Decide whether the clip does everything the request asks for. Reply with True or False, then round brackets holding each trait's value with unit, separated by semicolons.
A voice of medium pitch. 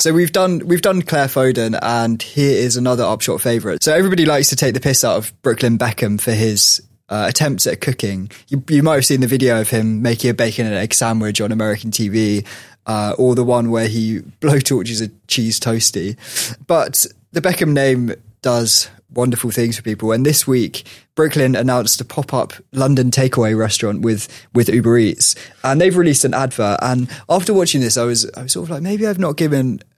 False (125 Hz)